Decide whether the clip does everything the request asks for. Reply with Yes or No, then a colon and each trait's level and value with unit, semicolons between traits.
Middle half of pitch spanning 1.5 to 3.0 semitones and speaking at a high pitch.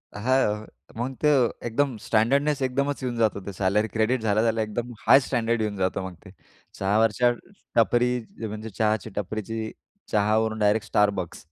No: narrow, 2.6 semitones; low, 110 Hz